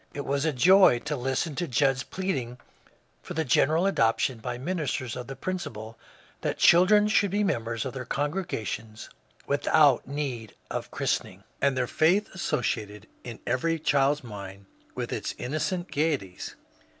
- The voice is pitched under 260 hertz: Yes, low, 135 Hz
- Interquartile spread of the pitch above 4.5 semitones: Yes, wide, 5.4 semitones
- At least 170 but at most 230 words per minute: No, average, 155 wpm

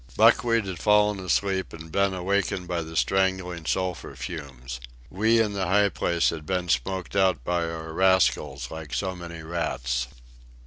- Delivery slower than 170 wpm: Yes, average, 160 wpm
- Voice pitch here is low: Yes, very low, 90 Hz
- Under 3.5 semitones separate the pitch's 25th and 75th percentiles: Yes, average, 3.1 semitones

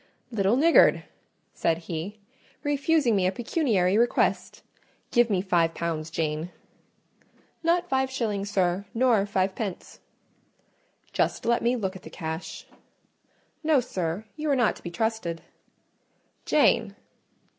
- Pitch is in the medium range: No, high, 205 Hz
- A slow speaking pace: Yes, slow, 125 wpm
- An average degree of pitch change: No, wide, 5.9 semitones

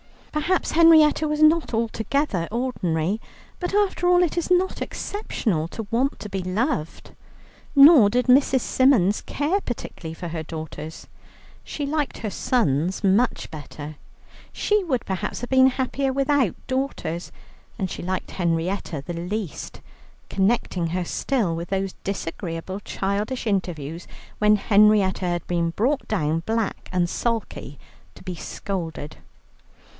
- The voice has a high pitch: Yes, high, 210 Hz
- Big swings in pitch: Yes, wide, 7.4 semitones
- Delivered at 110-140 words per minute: Yes, slow, 135 wpm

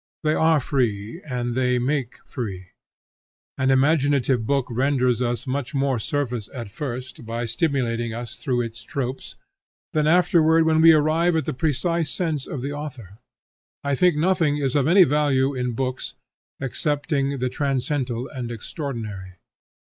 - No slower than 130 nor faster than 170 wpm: Yes, average, 150 wpm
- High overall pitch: No, low, 135 Hz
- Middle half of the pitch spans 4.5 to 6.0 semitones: No, average, 3.6 semitones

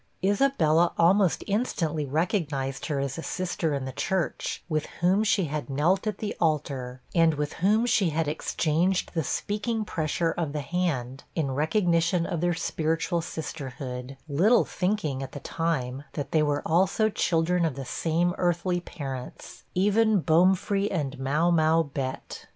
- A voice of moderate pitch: Yes, medium, 165 Hz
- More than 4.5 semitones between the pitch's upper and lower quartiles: No, average, 4.0 semitones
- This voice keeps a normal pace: Yes, average, 155 wpm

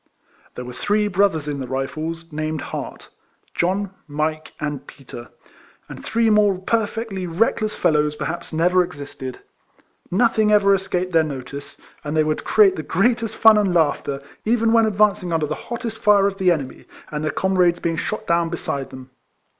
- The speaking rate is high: No, average, 180 wpm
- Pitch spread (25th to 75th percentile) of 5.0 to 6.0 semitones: Yes, average, 5.3 semitones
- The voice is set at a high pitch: No, medium, 175 Hz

